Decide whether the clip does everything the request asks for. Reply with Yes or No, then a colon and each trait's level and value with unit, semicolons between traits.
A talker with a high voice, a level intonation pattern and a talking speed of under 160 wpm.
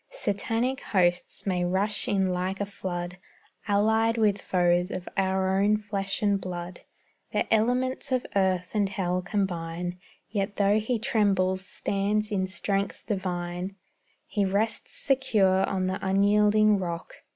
Yes: high, 195 Hz; narrow, 2.3 semitones; slow, 135 wpm